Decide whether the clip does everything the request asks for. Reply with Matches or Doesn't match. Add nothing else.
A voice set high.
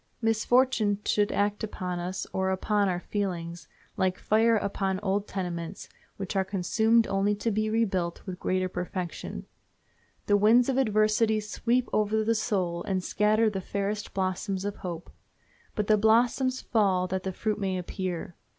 Matches